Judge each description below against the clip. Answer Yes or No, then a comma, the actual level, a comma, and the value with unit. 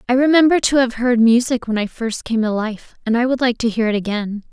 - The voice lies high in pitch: Yes, high, 235 Hz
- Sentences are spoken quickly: Yes, fast, 265 wpm